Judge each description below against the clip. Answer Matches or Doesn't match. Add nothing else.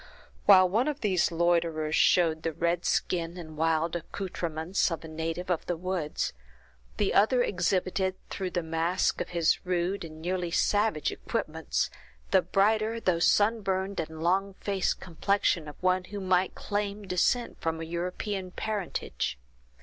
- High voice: Doesn't match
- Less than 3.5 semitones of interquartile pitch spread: Matches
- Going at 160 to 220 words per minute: Doesn't match